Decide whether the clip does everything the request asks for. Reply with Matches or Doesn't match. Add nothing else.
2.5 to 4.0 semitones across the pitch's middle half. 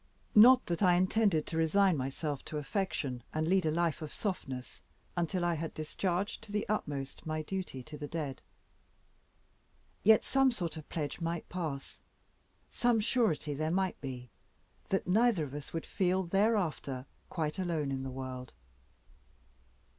Doesn't match